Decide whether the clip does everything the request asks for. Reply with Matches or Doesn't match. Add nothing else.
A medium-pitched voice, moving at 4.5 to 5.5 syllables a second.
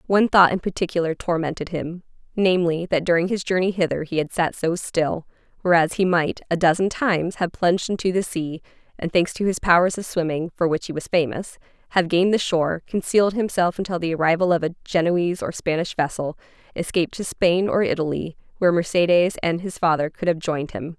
Doesn't match